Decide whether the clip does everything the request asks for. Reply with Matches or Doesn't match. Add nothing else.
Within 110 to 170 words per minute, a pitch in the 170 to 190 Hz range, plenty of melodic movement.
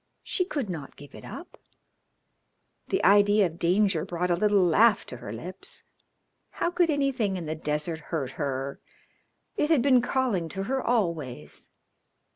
Matches